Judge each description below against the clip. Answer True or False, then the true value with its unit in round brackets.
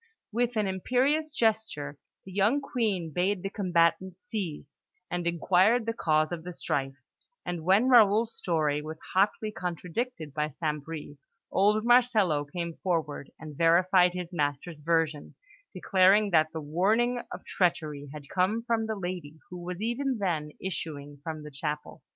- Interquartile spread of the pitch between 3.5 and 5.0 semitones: False (5.4 semitones)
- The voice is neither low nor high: True (180 Hz)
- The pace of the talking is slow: False (150 wpm)